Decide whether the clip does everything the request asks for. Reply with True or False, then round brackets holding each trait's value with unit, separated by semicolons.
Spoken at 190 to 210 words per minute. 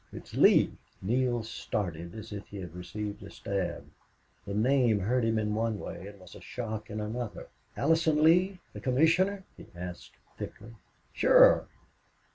False (155 wpm)